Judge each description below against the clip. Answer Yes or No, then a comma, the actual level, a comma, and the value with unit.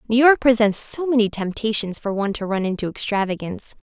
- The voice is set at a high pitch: Yes, high, 220 Hz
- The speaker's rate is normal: Yes, average, 185 wpm